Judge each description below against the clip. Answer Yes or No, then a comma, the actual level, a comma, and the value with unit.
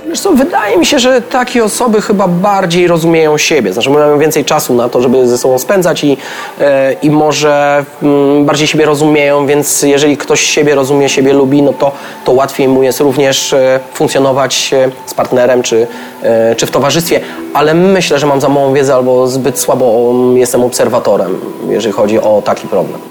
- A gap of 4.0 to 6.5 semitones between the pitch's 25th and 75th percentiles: No, average, 2.7 semitones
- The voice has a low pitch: No, medium, 145 Hz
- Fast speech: Yes, fast, 170 wpm